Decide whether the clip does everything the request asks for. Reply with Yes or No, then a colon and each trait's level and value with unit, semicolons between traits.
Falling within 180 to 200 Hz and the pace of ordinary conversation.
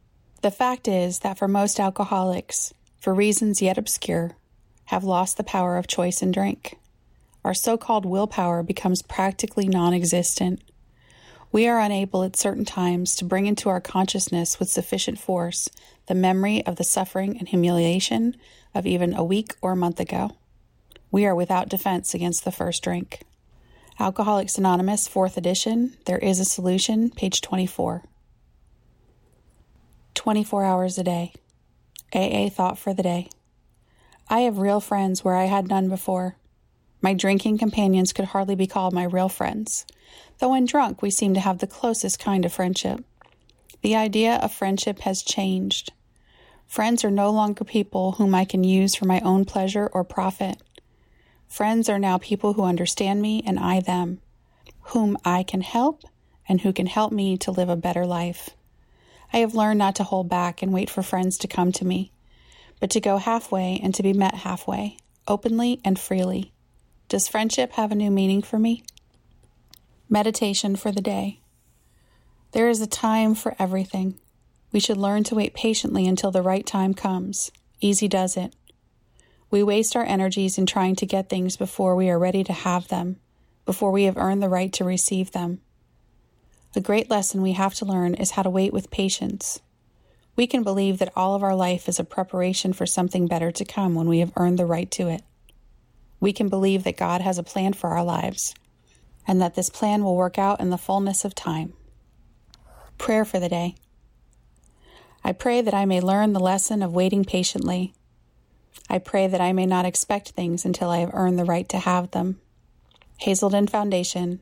Yes: high, 190 Hz; average, 175 wpm